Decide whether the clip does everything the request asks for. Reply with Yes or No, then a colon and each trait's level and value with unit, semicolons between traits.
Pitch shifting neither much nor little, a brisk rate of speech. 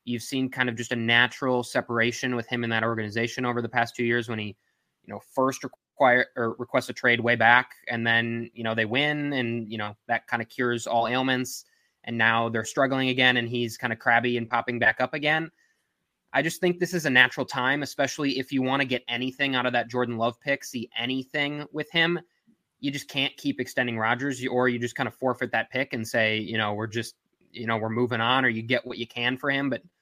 No: narrow, 2.2 semitones; fast, 240 wpm